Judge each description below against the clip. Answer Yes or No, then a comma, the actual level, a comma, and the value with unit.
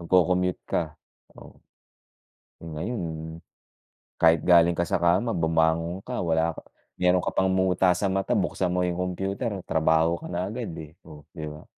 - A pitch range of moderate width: No, narrow, 2.3 semitones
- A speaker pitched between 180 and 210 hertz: No, very low, 85 Hz